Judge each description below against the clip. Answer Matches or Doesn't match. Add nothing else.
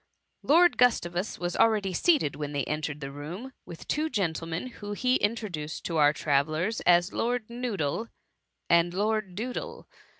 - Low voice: Doesn't match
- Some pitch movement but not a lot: Doesn't match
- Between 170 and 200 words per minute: Doesn't match